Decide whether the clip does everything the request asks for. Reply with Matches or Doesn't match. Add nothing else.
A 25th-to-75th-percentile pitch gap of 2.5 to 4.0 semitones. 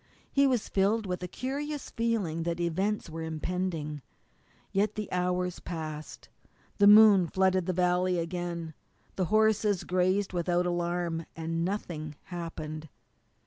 Matches